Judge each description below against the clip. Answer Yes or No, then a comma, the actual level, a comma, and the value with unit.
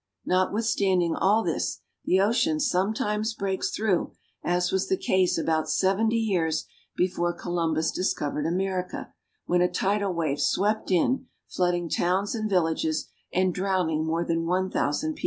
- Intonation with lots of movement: No, average, 2.9 semitones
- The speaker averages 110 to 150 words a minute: Yes, average, 140 wpm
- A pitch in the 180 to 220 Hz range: Yes, medium, 185 Hz